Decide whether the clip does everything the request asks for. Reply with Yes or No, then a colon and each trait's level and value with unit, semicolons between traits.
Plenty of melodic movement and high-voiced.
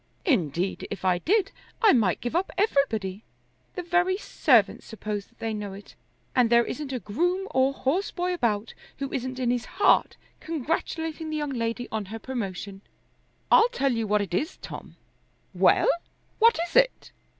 Yes: wide, 8.0 semitones; very high, 255 Hz